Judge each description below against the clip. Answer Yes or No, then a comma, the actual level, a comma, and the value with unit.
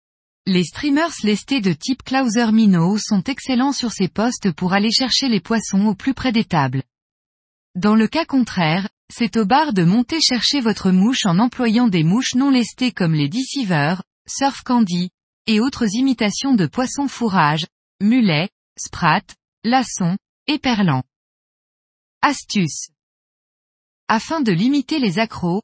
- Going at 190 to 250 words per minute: No, slow, 145 wpm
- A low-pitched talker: No, high, 220 Hz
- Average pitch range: No, wide, 5.7 semitones